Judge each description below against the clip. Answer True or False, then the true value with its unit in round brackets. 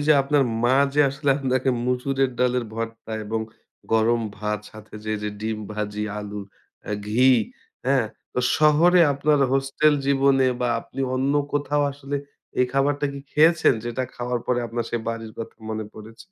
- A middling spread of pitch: True (3.7 semitones)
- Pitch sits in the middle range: False (125 Hz)